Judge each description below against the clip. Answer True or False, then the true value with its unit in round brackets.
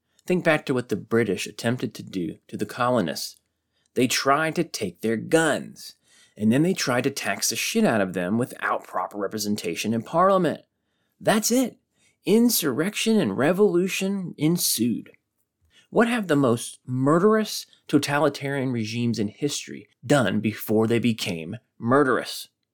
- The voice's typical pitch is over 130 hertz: True (140 Hz)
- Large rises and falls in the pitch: True (7.9 semitones)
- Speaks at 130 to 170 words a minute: True (145 wpm)